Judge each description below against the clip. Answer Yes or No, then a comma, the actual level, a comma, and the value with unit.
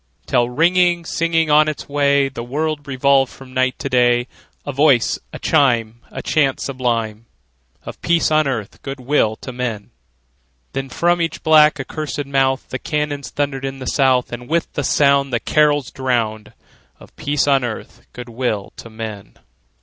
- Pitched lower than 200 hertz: Yes, low, 135 Hz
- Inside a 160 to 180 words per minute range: Yes, average, 165 wpm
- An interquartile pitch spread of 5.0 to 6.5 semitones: No, average, 3.4 semitones